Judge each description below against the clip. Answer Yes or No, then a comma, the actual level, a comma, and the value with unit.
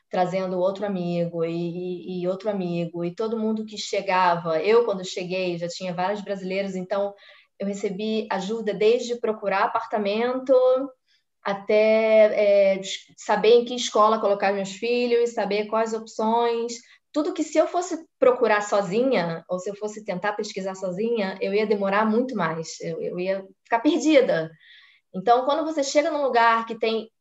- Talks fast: No, average, 155 wpm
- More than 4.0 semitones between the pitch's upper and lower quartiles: No, average, 3.5 semitones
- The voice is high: Yes, high, 210 Hz